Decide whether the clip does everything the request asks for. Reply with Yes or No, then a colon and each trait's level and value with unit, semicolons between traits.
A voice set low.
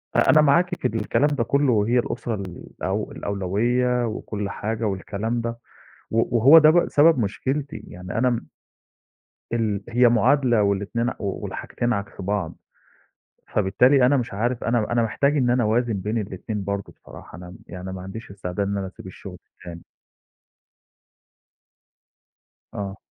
Yes: low, 110 Hz